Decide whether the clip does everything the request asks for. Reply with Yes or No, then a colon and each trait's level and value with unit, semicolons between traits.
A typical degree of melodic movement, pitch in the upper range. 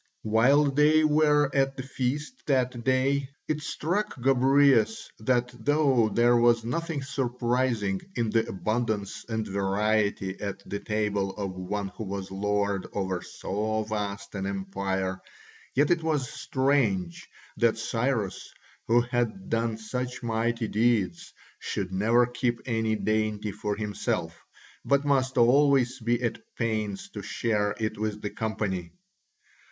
No: average, 4.2 semitones; low, 115 Hz